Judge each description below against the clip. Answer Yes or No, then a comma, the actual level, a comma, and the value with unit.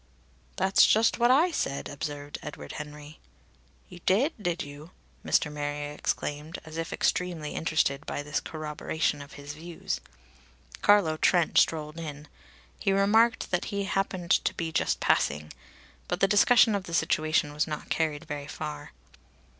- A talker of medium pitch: Yes, medium, 160 Hz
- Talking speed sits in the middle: Yes, average, 150 wpm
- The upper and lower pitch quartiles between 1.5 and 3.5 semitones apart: No, average, 4.3 semitones